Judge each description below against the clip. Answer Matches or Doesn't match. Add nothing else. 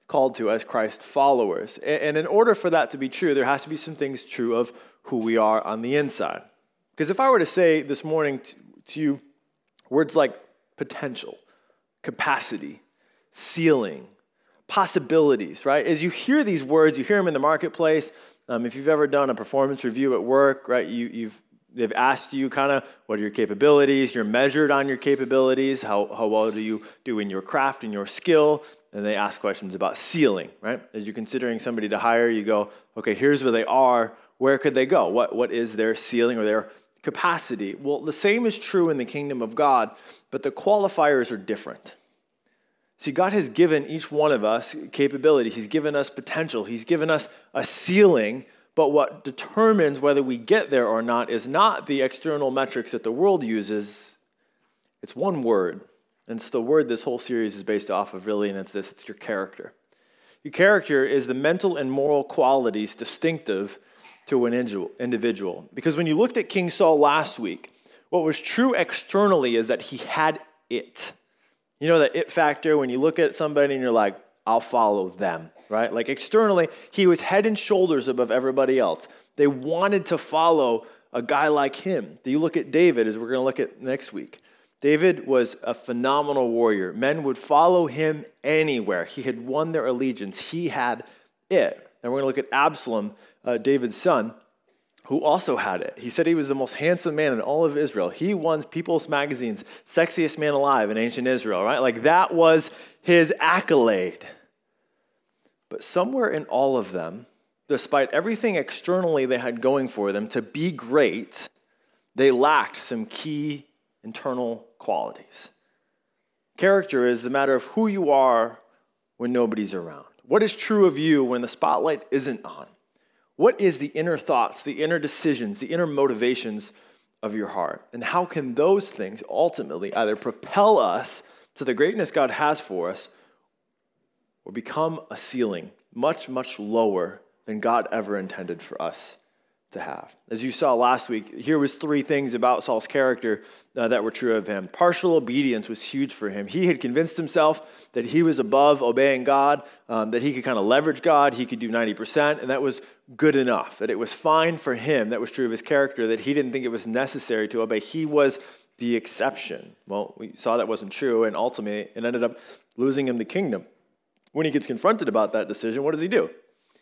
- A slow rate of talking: Doesn't match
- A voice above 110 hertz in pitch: Matches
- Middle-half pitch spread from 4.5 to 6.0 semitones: Matches